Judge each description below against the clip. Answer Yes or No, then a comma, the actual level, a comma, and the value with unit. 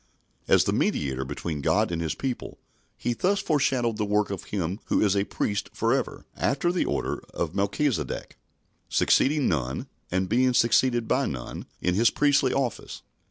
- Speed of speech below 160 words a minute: No, average, 165 wpm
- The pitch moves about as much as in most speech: No, wide, 6.5 semitones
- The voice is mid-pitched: No, low, 110 Hz